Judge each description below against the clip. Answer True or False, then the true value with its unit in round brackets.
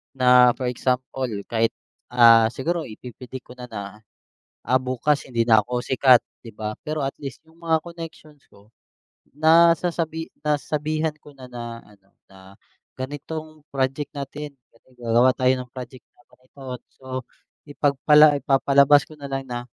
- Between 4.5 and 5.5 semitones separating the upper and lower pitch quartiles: False (3.4 semitones)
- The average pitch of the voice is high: False (135 Hz)